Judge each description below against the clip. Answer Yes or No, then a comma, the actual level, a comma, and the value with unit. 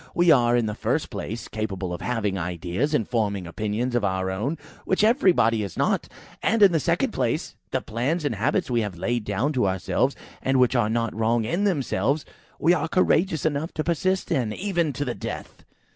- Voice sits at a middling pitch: No, low, 120 Hz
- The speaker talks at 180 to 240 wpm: Yes, average, 200 wpm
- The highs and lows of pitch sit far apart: Yes, wide, 6.9 semitones